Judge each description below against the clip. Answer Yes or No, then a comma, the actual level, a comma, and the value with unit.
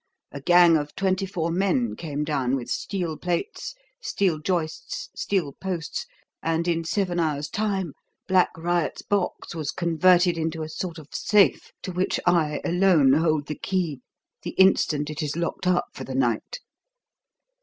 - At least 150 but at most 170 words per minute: Yes, average, 155 wpm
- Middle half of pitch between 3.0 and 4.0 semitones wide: Yes, average, 3.4 semitones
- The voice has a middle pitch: Yes, medium, 170 Hz